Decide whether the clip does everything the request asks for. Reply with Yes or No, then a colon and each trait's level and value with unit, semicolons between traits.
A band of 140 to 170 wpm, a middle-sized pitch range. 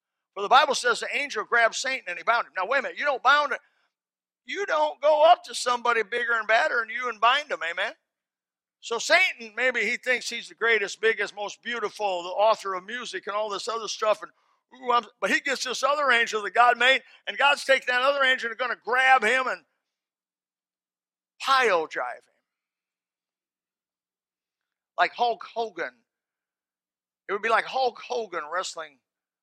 No: average, 185 wpm; average, 4.6 semitones